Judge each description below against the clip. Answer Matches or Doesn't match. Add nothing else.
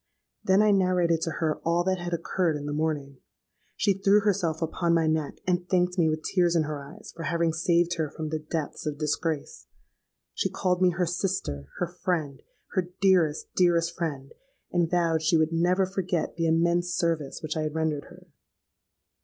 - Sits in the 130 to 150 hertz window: Doesn't match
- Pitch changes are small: Matches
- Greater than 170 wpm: Matches